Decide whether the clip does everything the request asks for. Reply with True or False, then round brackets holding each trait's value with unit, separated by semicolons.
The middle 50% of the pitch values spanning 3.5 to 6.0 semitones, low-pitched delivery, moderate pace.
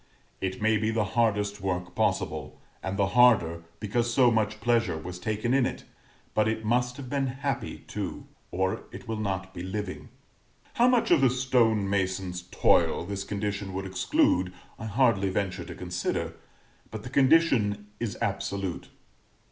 True (4.0 semitones; 105 Hz; 160 wpm)